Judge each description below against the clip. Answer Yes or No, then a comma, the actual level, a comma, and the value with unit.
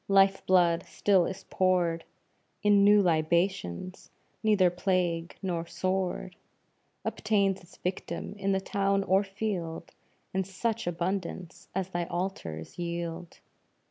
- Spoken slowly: Yes, slow, 115 wpm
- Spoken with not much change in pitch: Yes, narrow, 2.2 semitones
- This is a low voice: No, medium, 185 Hz